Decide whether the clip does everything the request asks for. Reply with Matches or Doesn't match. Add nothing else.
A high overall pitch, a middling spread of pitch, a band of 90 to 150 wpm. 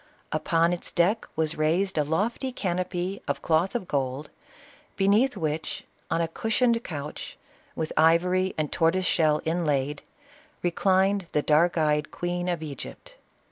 Doesn't match